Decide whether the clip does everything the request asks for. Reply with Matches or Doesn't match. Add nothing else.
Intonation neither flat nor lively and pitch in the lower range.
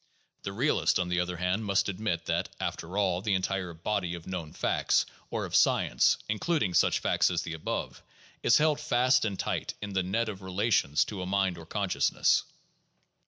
Matches